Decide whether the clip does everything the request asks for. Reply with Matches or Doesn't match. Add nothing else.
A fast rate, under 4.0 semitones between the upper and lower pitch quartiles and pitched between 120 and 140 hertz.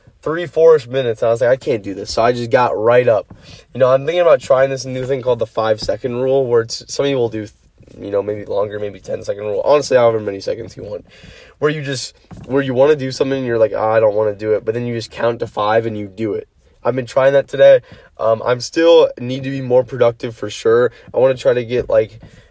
Doesn't match